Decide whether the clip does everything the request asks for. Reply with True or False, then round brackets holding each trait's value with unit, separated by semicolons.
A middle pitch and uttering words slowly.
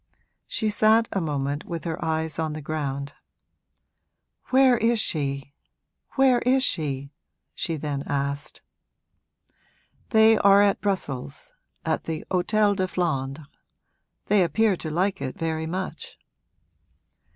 True (165 Hz; 120 wpm)